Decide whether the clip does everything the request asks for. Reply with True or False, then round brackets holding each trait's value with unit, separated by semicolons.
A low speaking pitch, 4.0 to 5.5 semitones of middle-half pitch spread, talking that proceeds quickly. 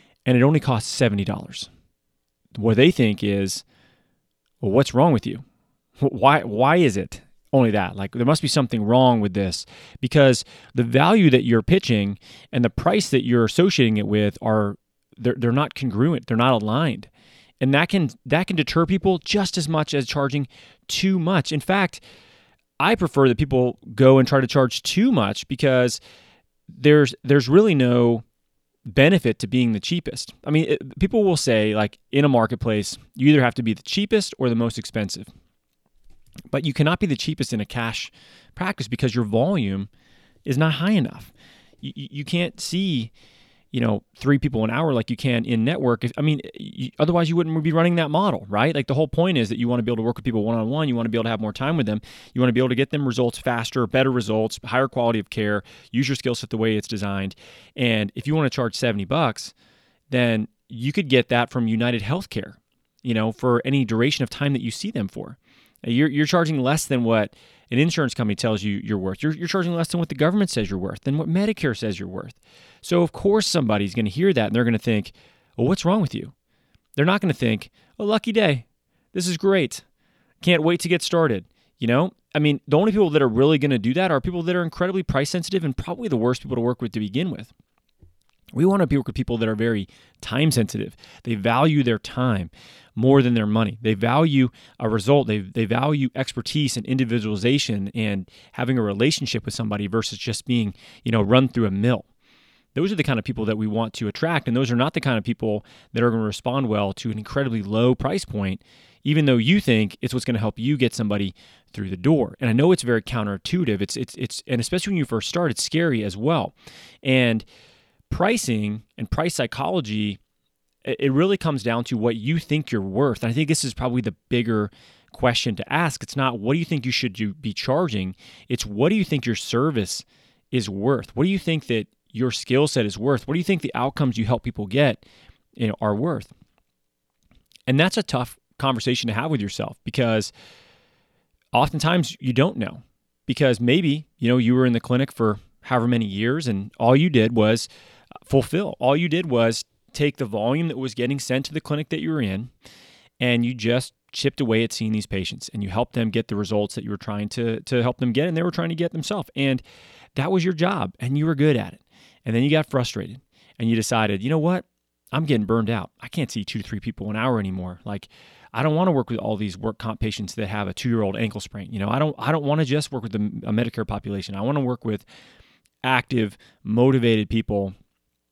True (125 Hz; 5.0 semitones; 225 wpm)